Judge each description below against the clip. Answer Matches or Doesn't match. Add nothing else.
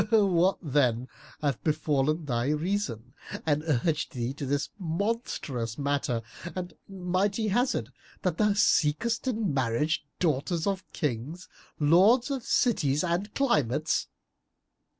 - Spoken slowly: Matches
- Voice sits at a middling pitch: Matches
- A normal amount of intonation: Doesn't match